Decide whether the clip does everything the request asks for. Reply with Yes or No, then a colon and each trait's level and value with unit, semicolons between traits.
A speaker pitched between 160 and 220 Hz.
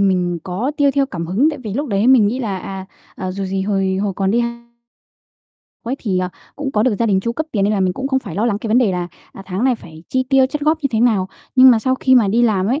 Yes: high, 215 Hz